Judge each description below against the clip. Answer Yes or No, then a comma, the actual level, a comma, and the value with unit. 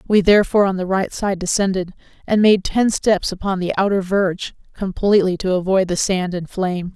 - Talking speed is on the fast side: No, average, 190 wpm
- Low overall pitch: No, high, 190 Hz